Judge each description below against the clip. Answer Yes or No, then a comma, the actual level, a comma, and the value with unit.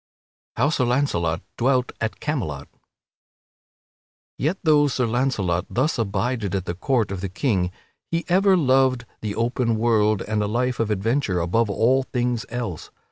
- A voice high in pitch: No, low, 115 Hz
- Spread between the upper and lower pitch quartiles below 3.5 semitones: No, average, 4.5 semitones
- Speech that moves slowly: No, average, 155 wpm